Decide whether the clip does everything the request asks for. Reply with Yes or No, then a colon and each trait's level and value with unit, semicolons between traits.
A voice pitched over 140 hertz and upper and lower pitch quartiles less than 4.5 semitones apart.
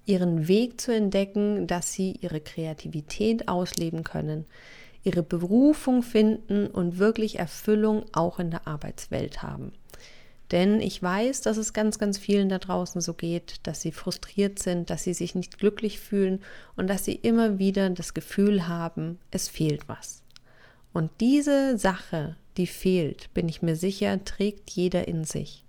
Yes: high, 190 Hz; average, 3.4 semitones